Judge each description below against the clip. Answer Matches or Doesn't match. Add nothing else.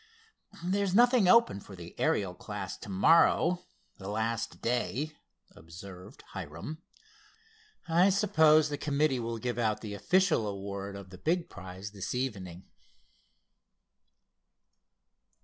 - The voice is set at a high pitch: Doesn't match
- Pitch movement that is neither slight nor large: Doesn't match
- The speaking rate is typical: Doesn't match